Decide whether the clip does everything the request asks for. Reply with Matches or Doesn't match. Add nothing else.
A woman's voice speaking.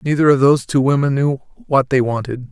Doesn't match